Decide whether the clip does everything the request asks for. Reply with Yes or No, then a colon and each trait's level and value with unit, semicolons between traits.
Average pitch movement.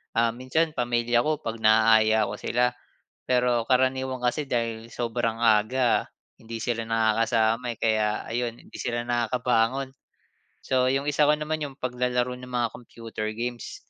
No: narrow, 1.9 semitones